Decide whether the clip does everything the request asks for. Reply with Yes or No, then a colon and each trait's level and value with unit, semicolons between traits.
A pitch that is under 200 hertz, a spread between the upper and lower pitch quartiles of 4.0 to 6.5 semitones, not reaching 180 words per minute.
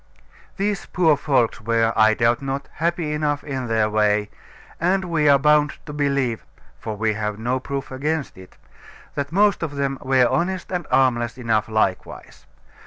Yes: low, 135 Hz; average, 5.0 semitones; average, 165 wpm